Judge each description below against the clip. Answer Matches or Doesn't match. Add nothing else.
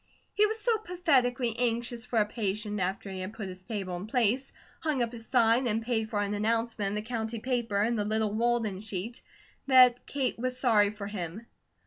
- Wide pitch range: Doesn't match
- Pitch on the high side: Matches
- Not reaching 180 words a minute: Doesn't match